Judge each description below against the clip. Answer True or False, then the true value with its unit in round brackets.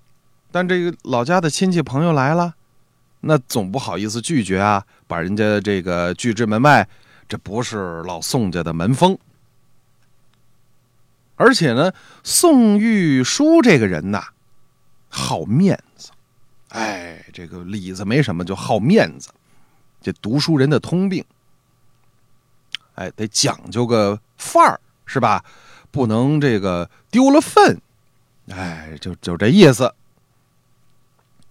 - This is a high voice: False (125 Hz)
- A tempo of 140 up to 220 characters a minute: True (180 characters per minute)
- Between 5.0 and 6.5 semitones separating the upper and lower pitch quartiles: True (5.6 semitones)